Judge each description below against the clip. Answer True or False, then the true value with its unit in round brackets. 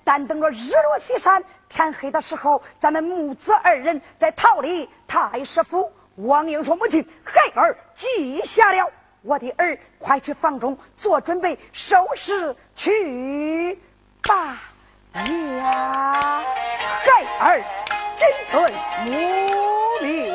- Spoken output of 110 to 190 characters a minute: True (160 characters per minute)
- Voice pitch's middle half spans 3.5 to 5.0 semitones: True (4.5 semitones)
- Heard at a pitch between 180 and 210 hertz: False (320 Hz)